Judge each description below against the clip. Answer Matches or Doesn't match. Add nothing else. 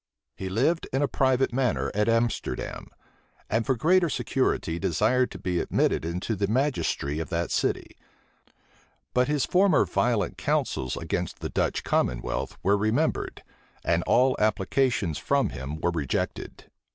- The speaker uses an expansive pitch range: Matches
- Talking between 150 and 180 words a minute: Doesn't match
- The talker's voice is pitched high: Doesn't match